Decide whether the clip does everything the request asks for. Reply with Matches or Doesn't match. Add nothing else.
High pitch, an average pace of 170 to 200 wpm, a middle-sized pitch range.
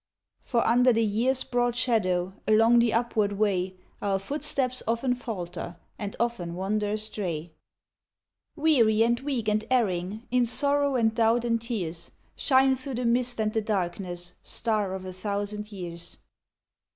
Doesn't match